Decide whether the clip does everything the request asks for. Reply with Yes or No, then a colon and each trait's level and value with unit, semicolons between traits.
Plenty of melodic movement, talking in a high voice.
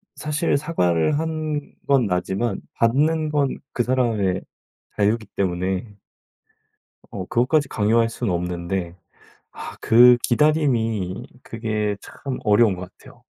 No: wide, 6.4 semitones; low, 115 Hz